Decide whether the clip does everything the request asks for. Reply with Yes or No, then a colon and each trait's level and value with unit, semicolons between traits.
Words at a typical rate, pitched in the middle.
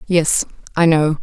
Yes: average, 145 wpm; medium, 160 Hz